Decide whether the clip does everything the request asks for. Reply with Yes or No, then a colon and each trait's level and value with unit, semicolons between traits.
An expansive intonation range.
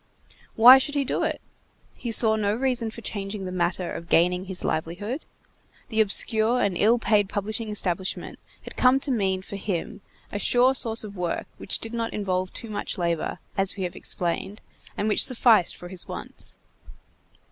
No: average, 3.5 semitones